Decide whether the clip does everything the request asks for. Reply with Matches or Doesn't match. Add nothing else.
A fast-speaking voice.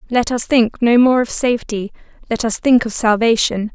Doesn't match